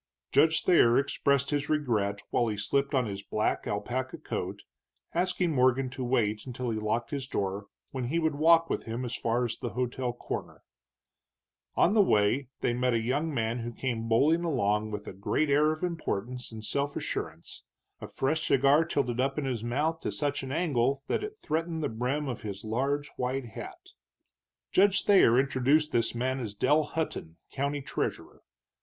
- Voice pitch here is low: Yes, low, 130 Hz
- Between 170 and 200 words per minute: Yes, average, 180 wpm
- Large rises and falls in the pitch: No, average, 4.3 semitones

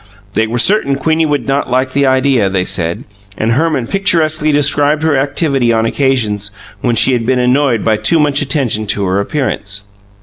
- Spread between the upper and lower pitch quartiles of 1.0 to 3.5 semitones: No, average, 4.5 semitones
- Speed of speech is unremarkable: Yes, average, 180 wpm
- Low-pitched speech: Yes, low, 130 Hz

